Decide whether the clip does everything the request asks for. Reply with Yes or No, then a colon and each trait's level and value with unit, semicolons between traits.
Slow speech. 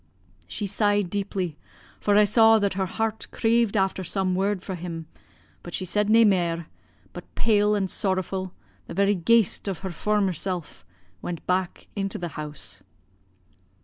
No: average, 155 wpm